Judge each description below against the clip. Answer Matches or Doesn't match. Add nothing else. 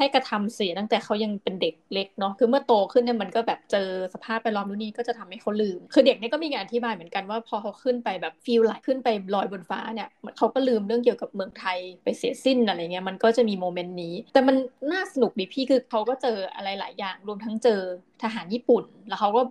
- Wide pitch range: Doesn't match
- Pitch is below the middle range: Doesn't match